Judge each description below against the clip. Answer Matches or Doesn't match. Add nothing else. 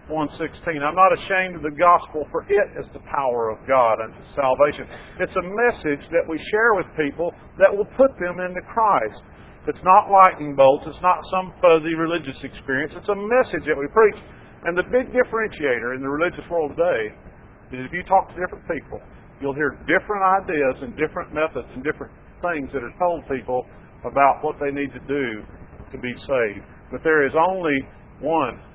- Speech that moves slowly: Doesn't match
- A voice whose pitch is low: Doesn't match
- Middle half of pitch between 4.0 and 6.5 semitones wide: Matches